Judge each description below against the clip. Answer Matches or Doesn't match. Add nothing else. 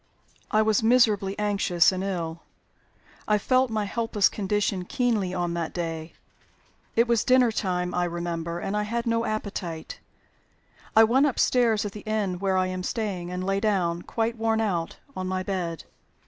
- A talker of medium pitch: Doesn't match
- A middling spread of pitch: Matches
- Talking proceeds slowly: Doesn't match